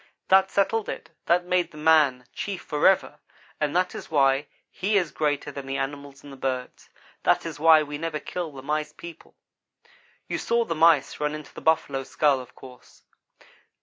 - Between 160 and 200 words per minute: Yes, average, 180 wpm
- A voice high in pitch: No, medium, 150 Hz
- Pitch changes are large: No, average, 3.4 semitones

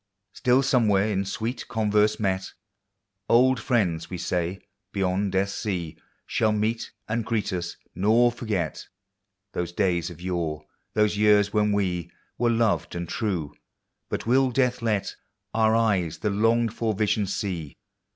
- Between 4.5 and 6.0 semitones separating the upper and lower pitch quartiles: No, average, 3.7 semitones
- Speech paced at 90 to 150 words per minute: Yes, average, 140 wpm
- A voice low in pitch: Yes, low, 105 Hz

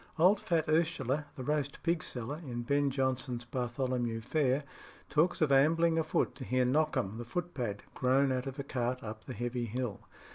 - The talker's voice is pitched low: Yes, low, 130 Hz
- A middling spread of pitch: Yes, average, 3.8 semitones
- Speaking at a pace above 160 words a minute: Yes, average, 175 wpm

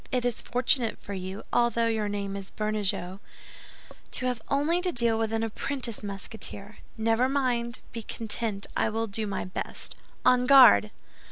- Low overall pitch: No, high, 225 Hz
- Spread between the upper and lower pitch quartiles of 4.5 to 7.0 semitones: No, average, 3.1 semitones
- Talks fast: No, average, 160 wpm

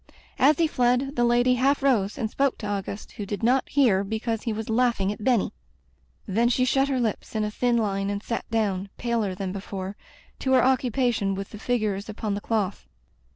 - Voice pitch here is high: Yes, high, 225 Hz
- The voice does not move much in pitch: No, average, 3.7 semitones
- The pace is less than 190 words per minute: No, average, 200 wpm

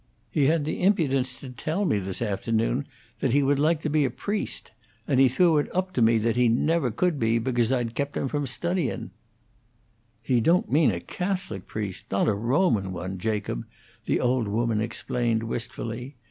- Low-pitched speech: Yes, low, 125 Hz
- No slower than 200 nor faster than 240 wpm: No, average, 190 wpm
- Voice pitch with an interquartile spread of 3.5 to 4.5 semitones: No, average, 5.0 semitones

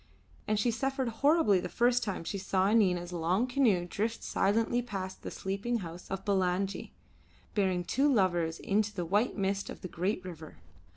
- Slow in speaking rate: No, average, 175 wpm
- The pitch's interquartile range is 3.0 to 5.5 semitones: Yes, average, 3.9 semitones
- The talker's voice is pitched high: Yes, high, 195 Hz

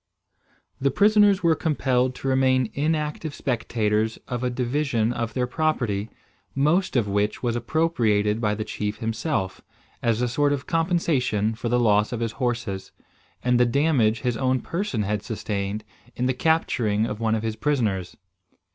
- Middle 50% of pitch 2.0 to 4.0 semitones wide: No, average, 4.5 semitones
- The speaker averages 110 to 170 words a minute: Yes, average, 160 wpm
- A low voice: Yes, low, 120 Hz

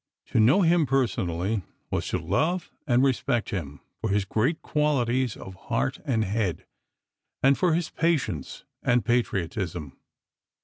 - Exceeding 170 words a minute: No, slow, 135 wpm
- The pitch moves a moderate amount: No, wide, 6.1 semitones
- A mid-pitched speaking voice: No, low, 120 Hz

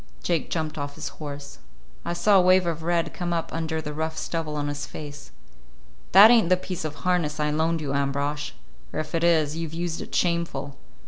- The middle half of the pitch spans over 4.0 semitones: No, narrow, 2.6 semitones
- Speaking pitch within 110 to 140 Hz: No, medium, 160 Hz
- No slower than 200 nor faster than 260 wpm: Yes, fast, 205 wpm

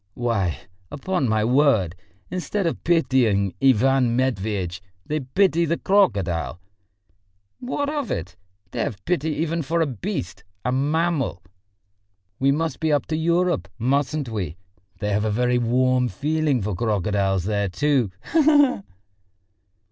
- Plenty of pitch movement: Yes, wide, 7.5 semitones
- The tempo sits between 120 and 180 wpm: Yes, average, 140 wpm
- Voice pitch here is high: No, low, 130 Hz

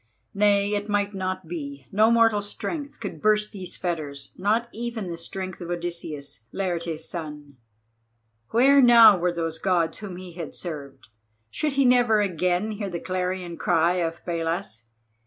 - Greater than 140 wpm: Yes, average, 155 wpm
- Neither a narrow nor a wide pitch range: Yes, average, 4.0 semitones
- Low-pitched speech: No, medium, 185 Hz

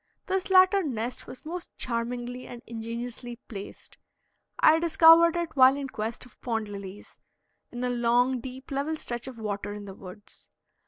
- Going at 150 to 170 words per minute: Yes, average, 160 wpm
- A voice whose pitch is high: Yes, high, 245 Hz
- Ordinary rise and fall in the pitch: Yes, average, 4.4 semitones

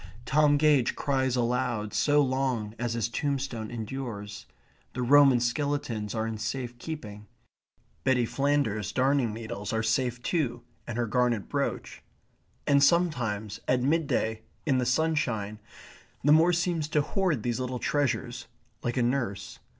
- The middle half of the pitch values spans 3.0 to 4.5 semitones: Yes, average, 4.2 semitones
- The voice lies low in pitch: Yes, low, 125 Hz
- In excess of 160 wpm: No, average, 140 wpm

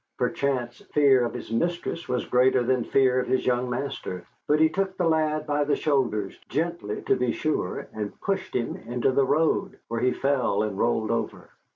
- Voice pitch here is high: No, low, 130 Hz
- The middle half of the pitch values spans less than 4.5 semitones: Yes, average, 4.1 semitones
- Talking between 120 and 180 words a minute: No, average, 190 wpm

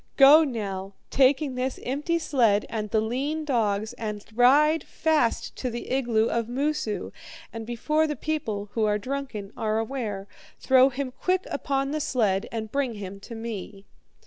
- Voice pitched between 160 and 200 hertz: No, high, 240 Hz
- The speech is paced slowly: No, average, 160 wpm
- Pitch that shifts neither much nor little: Yes, average, 4.5 semitones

